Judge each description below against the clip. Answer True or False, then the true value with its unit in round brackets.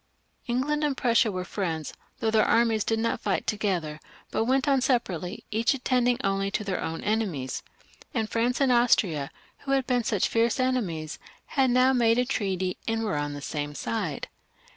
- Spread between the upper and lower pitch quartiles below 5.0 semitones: False (5.3 semitones)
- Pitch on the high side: True (225 Hz)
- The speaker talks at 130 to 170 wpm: False (180 wpm)